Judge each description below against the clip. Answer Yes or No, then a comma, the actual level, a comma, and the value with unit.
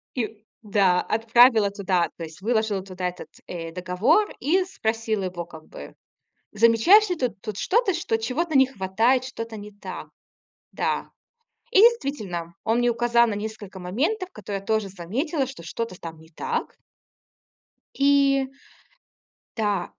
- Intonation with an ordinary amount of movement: No, wide, 5.7 semitones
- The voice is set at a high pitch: Yes, high, 220 Hz